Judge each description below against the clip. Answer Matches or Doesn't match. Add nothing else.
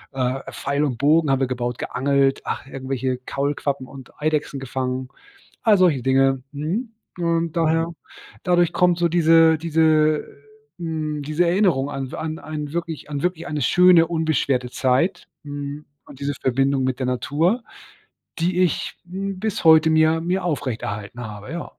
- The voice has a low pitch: Doesn't match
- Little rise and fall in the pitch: Doesn't match